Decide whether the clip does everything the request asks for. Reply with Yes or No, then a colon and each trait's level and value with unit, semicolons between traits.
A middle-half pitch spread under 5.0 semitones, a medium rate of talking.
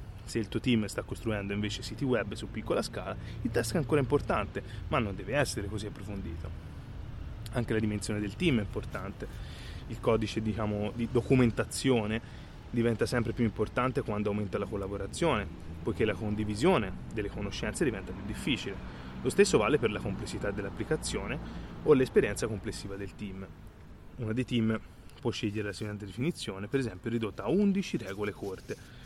Yes: narrow, 2.6 semitones; average, 160 wpm